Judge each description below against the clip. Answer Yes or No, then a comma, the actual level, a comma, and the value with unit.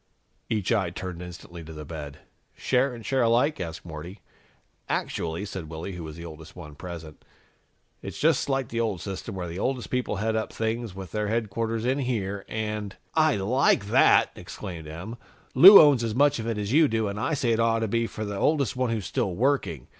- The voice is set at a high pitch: No, low, 105 Hz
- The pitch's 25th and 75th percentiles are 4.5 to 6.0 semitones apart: Yes, average, 5.2 semitones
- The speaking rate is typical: No, fast, 210 wpm